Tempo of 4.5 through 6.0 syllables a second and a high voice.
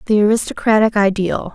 Yes: 5.8 syllables/s; high, 210 Hz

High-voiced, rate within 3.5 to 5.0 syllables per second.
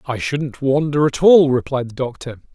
No: low, 135 Hz; 4.7 syllables/s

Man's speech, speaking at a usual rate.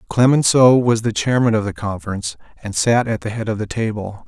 No: male; fast, 210 wpm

